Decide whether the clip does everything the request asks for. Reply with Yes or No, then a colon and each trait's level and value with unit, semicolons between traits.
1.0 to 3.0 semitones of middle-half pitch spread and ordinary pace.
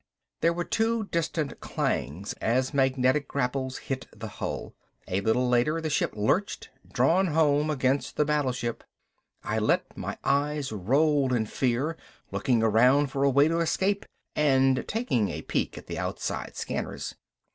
No: average, 3.6 semitones; average, 150 wpm